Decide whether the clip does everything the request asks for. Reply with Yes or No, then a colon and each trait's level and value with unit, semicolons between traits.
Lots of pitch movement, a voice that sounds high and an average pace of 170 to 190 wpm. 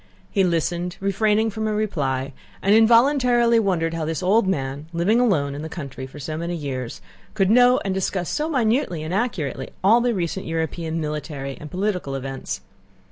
No: wide, 6.2 semitones; medium, 180 Hz; average, 175 wpm